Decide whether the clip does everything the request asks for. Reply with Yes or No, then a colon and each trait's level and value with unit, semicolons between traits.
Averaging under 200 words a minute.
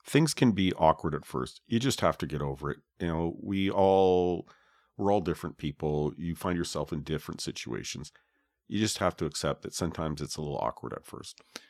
No: fast, 205 wpm